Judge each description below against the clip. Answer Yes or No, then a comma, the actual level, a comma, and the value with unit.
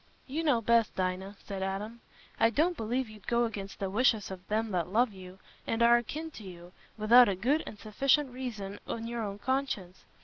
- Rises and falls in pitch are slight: No, average, 4.0 semitones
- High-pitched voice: Yes, high, 220 Hz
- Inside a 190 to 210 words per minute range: Yes, average, 200 wpm